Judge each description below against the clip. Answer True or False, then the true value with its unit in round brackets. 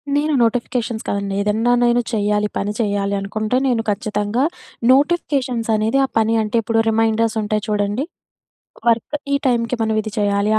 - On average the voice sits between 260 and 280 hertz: False (220 Hz)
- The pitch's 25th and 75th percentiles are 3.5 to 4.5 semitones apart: False (2.4 semitones)